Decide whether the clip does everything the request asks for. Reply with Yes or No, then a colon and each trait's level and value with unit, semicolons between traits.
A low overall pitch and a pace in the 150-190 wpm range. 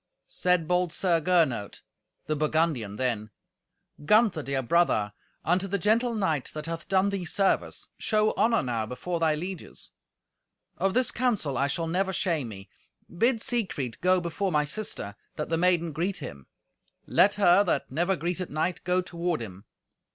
No: medium, 170 Hz; average, 160 wpm